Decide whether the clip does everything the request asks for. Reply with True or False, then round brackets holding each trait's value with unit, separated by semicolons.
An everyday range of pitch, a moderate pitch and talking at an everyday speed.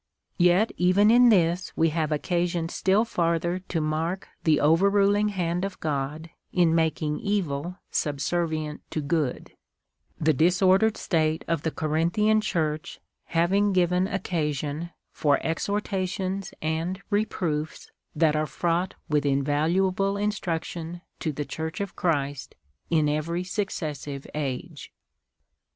False (3.5 semitones; 170 Hz; 125 wpm)